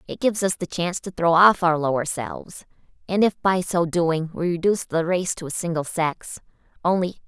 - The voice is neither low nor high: Yes, medium, 175 Hz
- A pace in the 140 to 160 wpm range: No, fast, 205 wpm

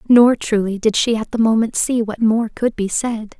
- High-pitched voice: Yes, high, 225 Hz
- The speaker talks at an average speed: No, fast, 230 wpm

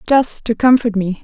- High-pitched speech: Yes, high, 225 Hz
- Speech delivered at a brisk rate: No, average, 195 wpm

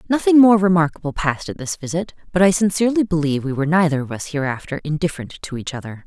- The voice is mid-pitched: Yes, medium, 165 Hz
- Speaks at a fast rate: Yes, fast, 210 wpm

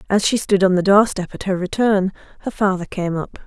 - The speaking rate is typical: No, fast, 245 wpm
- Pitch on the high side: Yes, high, 195 Hz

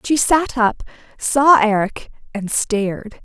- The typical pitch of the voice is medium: No, high, 235 Hz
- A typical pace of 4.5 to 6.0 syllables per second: No, 3.6 syllables/s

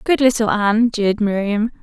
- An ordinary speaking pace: Yes, average, 165 wpm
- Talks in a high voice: Yes, high, 220 Hz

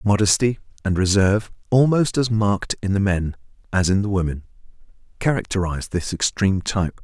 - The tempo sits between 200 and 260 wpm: No, average, 145 wpm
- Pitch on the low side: Yes, low, 100 Hz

